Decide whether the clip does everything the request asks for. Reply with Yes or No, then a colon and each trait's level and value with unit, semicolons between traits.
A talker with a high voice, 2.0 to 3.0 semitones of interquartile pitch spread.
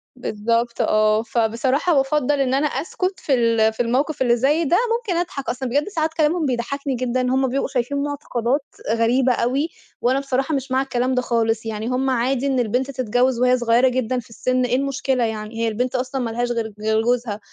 Yes: very high, 255 Hz; average, 2.7 semitones